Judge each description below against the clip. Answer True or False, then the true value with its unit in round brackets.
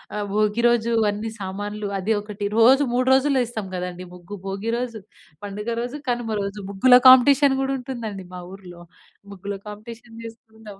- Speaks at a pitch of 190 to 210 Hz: False (220 Hz)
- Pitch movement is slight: False (3.0 semitones)